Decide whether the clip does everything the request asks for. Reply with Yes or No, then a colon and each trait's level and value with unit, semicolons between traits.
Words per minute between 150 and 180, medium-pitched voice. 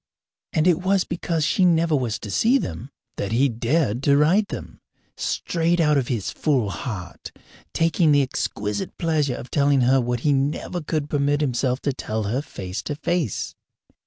Yes: average, 175 wpm; medium, 145 Hz